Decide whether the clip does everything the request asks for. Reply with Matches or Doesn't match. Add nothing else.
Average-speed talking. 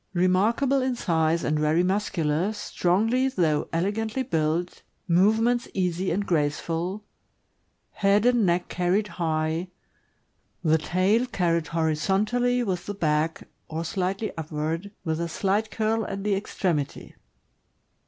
Doesn't match